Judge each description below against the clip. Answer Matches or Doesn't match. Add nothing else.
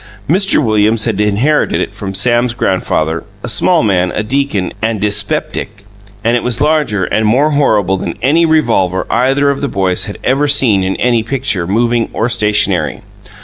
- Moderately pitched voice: Doesn't match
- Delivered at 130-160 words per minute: Doesn't match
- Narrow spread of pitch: Doesn't match